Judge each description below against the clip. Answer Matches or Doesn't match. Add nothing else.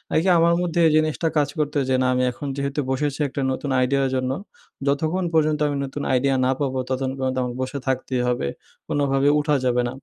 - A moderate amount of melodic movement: Doesn't match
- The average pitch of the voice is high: Doesn't match